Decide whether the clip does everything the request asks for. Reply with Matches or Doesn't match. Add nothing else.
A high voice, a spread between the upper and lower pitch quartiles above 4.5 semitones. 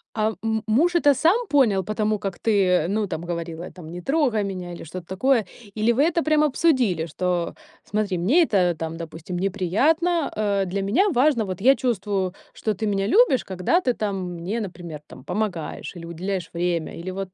Matches